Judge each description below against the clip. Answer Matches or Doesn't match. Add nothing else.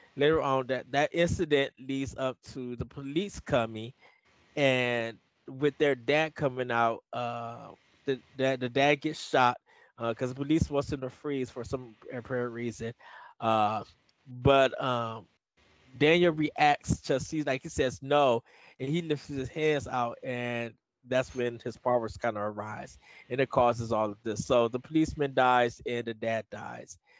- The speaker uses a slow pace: Doesn't match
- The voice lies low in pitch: Matches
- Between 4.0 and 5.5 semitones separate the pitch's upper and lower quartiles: Doesn't match